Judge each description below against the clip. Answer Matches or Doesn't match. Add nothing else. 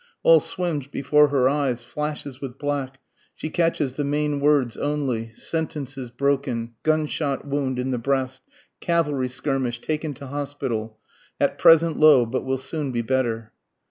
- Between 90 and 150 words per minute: Matches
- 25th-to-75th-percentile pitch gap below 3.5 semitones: Matches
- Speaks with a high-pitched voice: Doesn't match